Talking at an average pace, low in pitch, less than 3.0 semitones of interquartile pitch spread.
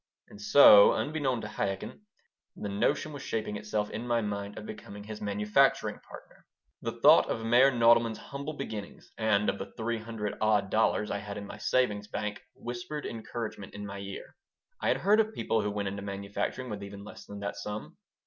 Yes: average, 190 wpm; low, 105 Hz; narrow, 2.5 semitones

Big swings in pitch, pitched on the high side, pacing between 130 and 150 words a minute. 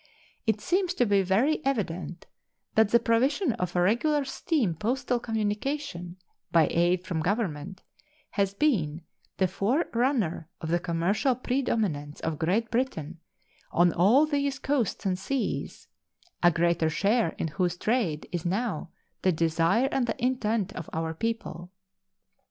Yes: wide, 6.3 semitones; high, 200 Hz; slow, 135 wpm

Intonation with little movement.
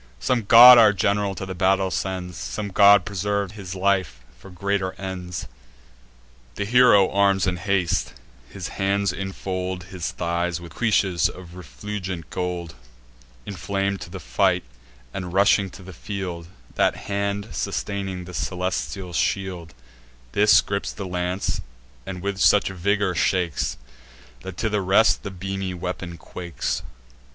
Yes: narrow, 2.0 semitones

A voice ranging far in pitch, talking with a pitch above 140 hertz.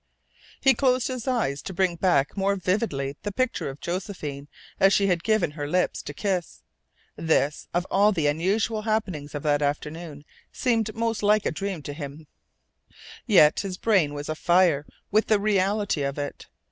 Yes: wide, 6.2 semitones; medium, 185 Hz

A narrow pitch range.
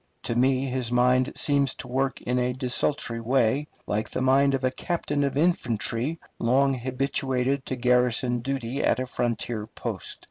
Yes: narrow, 1.8 semitones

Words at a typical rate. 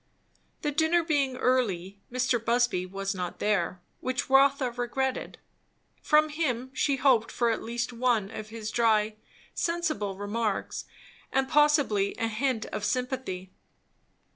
No: slow, 130 wpm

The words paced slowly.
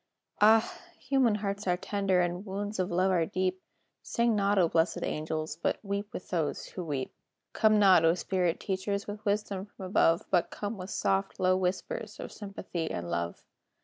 No: average, 180 wpm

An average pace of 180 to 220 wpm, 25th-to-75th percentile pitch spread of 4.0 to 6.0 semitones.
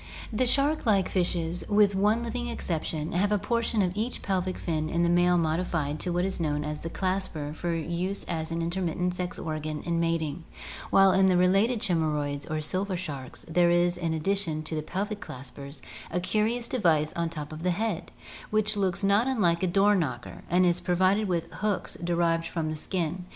No: fast, 205 wpm; average, 3.4 semitones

